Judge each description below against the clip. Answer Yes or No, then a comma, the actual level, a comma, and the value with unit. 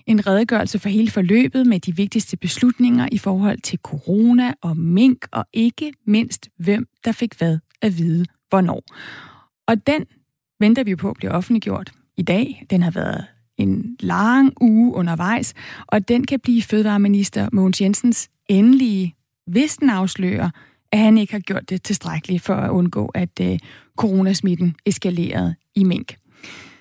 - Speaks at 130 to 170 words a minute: Yes, average, 150 wpm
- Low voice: No, high, 200 Hz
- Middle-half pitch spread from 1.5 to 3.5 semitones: No, average, 4.3 semitones